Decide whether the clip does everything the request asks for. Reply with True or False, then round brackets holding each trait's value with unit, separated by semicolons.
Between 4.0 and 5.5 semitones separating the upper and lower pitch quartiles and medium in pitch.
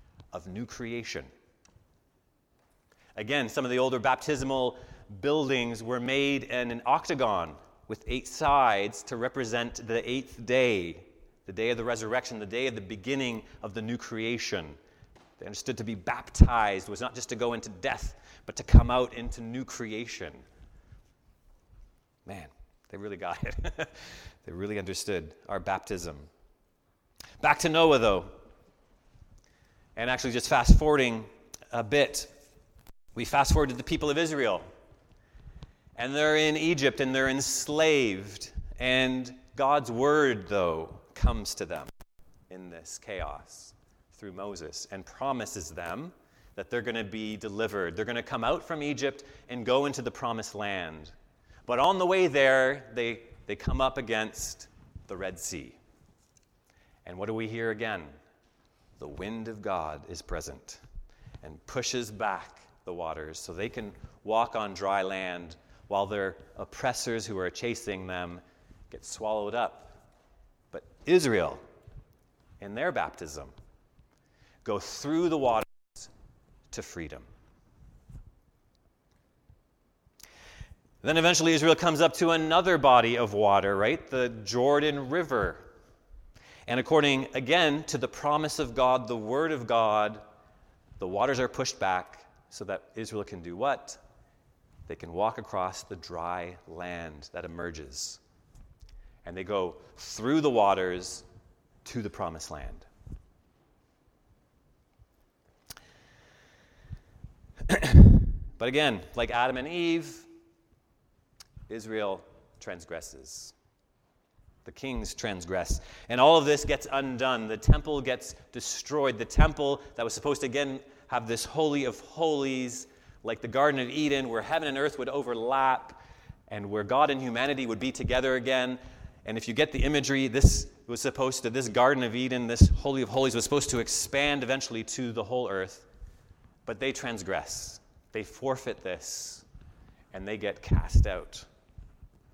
False (4.6 semitones; 120 Hz)